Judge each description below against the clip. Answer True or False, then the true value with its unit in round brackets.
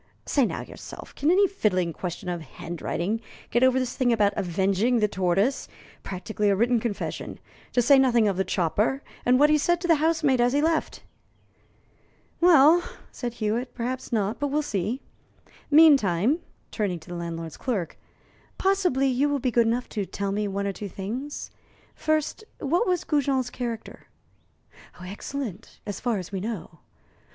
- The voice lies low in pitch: False (235 Hz)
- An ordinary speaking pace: True (165 wpm)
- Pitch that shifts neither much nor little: False (6.0 semitones)